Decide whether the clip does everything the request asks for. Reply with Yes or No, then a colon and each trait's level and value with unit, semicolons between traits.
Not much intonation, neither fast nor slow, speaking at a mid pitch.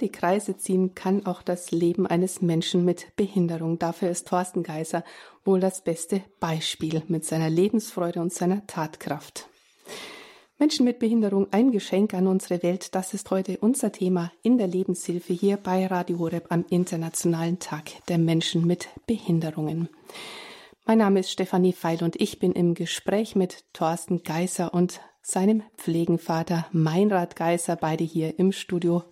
Yes: narrow, 2.2 semitones; average, 155 wpm; medium, 180 Hz